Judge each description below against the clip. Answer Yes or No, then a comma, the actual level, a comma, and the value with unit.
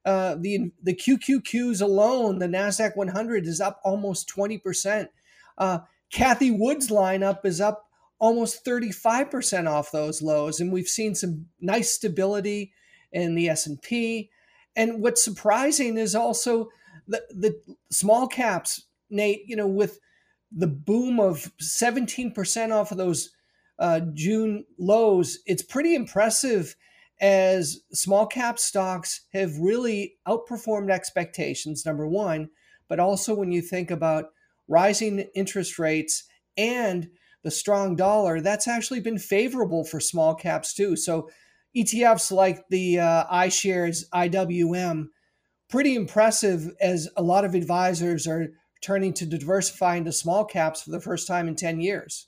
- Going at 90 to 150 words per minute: Yes, slow, 135 wpm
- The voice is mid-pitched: No, high, 195 Hz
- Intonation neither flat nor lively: Yes, average, 3.8 semitones